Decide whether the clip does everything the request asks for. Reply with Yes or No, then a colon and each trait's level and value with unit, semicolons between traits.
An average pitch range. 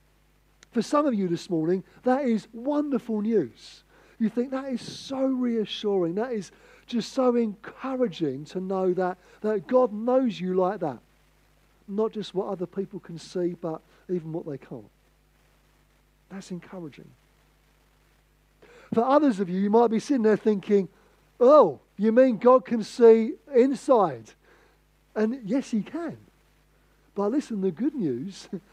Yes: average, 4.9 semitones